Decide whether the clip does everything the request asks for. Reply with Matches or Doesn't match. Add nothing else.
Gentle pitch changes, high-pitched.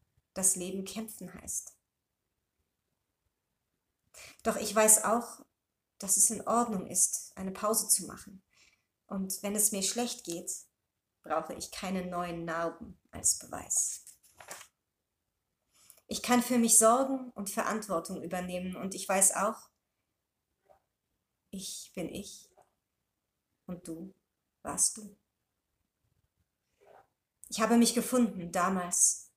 Doesn't match